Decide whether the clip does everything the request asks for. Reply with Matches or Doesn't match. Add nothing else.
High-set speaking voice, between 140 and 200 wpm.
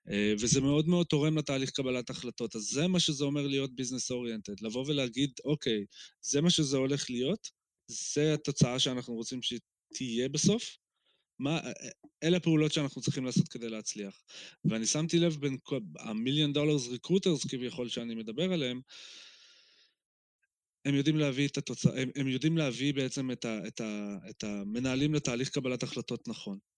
Doesn't match